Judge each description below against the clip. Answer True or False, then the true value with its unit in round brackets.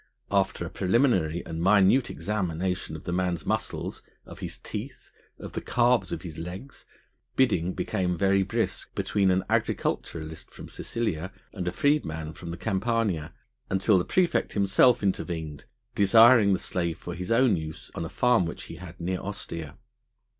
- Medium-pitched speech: False (95 Hz)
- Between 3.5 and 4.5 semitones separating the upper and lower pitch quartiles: True (3.9 semitones)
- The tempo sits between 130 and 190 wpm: True (160 wpm)